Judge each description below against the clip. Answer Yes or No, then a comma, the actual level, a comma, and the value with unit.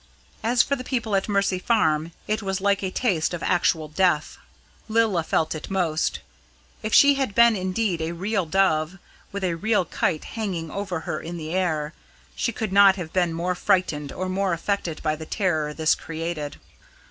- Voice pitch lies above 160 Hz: Yes, medium, 185 Hz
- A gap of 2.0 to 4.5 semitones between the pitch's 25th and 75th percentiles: Yes, average, 3.9 semitones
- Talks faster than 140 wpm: Yes, average, 180 wpm